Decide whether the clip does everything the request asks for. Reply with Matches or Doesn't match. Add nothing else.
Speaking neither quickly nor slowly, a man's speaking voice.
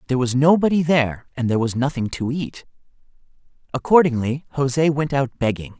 Matches